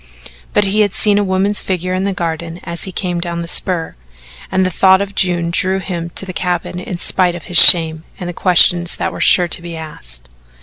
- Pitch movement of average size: No, narrow, 1.8 semitones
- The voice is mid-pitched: Yes, medium, 180 Hz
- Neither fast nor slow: No, fast, 225 wpm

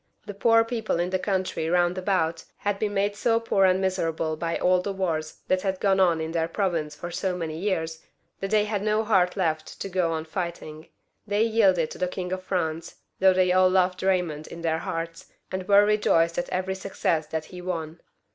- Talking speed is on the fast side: Yes, fast, 210 wpm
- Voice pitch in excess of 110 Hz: Yes, medium, 185 Hz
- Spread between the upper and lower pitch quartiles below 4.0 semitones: Yes, average, 2.9 semitones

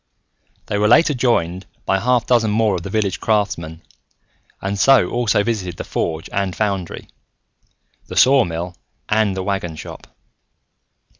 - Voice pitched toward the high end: No, low, 100 Hz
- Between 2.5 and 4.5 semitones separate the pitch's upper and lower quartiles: Yes, average, 3.7 semitones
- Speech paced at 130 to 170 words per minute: Yes, average, 145 wpm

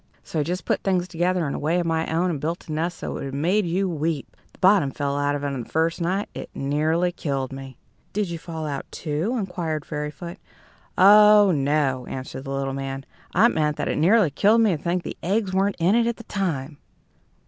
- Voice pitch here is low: No, medium, 165 Hz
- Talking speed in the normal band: No, fast, 225 wpm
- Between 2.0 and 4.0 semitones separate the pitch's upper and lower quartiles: No, average, 4.5 semitones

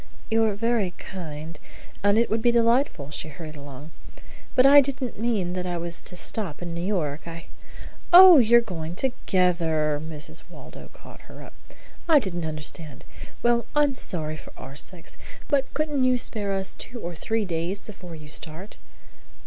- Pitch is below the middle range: No, medium, 185 Hz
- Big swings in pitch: Yes, wide, 6.7 semitones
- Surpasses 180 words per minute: No, average, 175 wpm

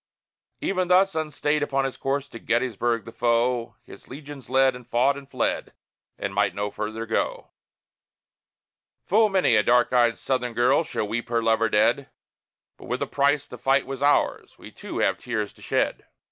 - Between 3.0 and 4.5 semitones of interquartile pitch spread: Yes, average, 3.4 semitones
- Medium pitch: No, low, 125 Hz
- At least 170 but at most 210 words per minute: Yes, average, 175 wpm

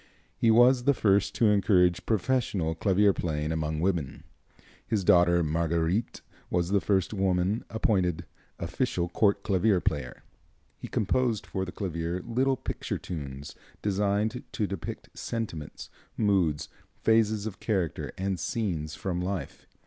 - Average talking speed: No, slow, 130 wpm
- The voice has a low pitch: Yes, very low, 95 Hz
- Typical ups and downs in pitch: Yes, average, 4.1 semitones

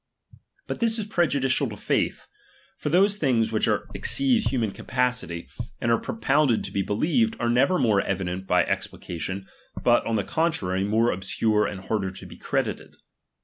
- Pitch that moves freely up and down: Yes, wide, 7.8 semitones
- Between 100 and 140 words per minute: No, average, 165 wpm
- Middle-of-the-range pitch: No, low, 115 Hz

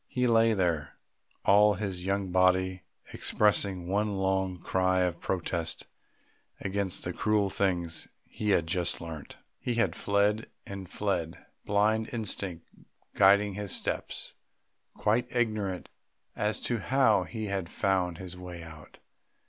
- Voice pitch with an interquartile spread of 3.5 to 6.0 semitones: No, average, 2.7 semitones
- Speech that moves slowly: Yes, slow, 130 wpm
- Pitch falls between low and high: No, very low, 95 Hz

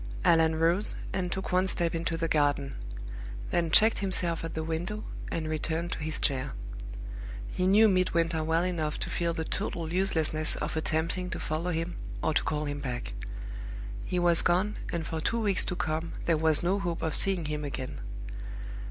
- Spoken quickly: No, average, 180 wpm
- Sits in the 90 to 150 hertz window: No, medium, 165 Hz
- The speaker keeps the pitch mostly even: Yes, narrow, 2.3 semitones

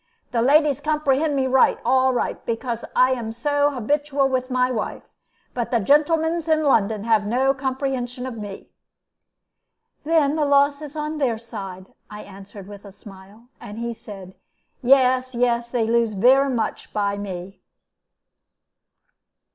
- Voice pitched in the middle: No, very high, 250 Hz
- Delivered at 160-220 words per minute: No, average, 145 wpm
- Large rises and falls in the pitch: No, average, 4.2 semitones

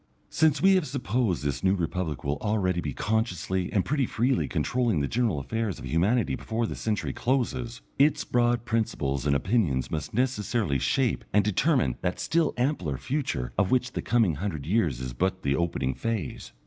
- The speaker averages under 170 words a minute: No, average, 175 wpm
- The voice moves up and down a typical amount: No, wide, 7.1 semitones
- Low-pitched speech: Yes, low, 105 Hz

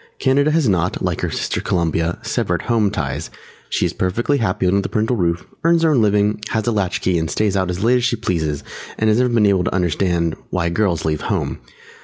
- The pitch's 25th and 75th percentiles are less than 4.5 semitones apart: No, average, 4.8 semitones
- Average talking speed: No, fast, 225 wpm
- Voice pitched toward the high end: No, low, 100 Hz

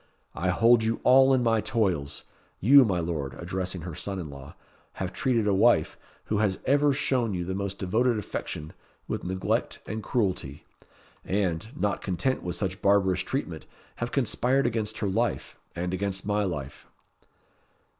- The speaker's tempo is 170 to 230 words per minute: No, average, 160 wpm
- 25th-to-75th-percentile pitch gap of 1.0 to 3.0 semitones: No, average, 4.2 semitones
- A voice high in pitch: No, low, 100 Hz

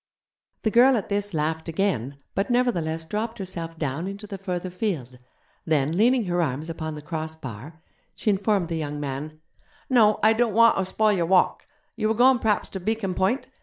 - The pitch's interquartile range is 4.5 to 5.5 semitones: Yes, average, 5.2 semitones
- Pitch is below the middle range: No, medium, 185 Hz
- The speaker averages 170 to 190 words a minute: Yes, average, 185 wpm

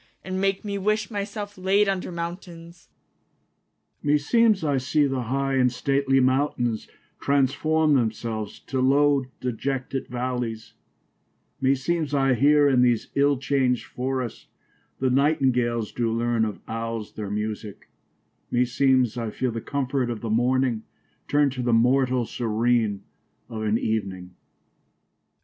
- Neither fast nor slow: Yes, average, 150 wpm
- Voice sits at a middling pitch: No, low, 130 Hz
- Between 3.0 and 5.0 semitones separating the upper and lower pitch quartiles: Yes, average, 3.7 semitones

